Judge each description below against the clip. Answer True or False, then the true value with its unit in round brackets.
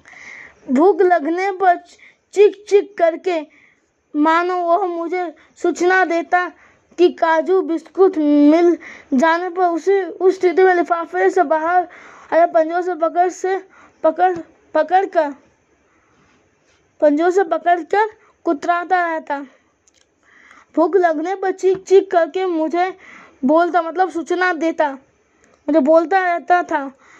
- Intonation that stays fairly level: True (2.2 semitones)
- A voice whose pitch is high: True (350 Hz)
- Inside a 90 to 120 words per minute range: True (115 wpm)